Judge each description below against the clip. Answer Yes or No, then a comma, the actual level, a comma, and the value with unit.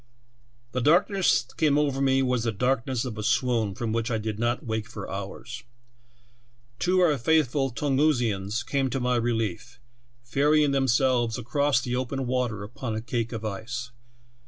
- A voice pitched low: Yes, low, 125 Hz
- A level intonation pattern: No, average, 3.0 semitones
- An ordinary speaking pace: Yes, average, 170 wpm